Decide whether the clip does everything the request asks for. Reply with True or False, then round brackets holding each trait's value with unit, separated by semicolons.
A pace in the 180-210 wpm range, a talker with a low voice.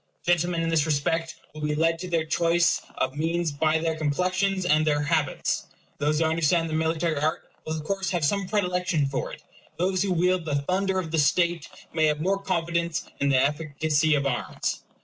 False (195 wpm; 165 Hz)